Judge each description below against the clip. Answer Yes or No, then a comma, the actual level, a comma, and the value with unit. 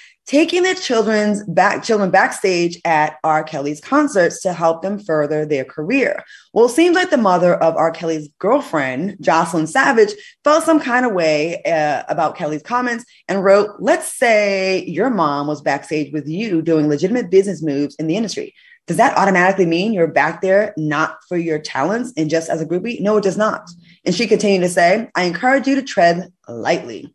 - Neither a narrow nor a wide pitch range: No, wide, 6.8 semitones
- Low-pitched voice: No, medium, 185 Hz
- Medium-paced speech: Yes, average, 190 wpm